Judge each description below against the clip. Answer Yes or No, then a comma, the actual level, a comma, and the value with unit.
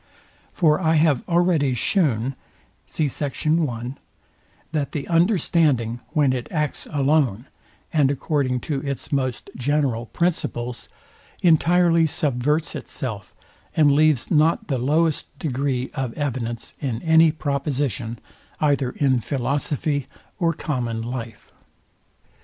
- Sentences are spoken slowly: Yes, slow, 105 wpm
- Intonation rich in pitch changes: No, average, 3.8 semitones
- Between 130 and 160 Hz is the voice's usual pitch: Yes, medium, 140 Hz